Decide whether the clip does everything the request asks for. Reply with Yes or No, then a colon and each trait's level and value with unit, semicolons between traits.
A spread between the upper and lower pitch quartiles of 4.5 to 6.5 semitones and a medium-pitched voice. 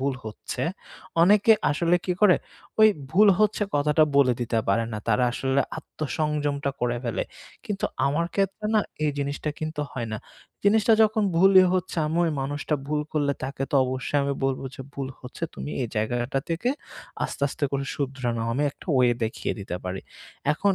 Yes: average, 5.3 semitones; medium, 145 Hz